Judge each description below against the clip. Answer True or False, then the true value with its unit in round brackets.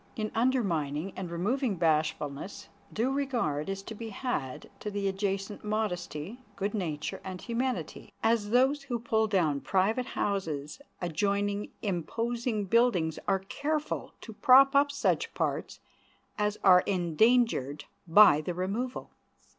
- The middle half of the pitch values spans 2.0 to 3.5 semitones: False (5.1 semitones)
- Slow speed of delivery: True (130 wpm)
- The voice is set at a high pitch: True (205 Hz)